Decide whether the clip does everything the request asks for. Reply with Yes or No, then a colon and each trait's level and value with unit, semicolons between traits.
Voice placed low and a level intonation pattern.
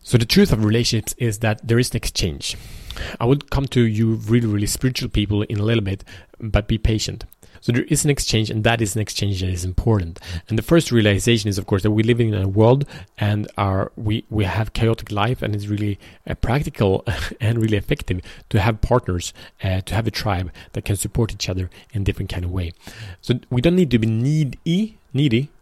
No: low, 110 Hz; average, 3.3 semitones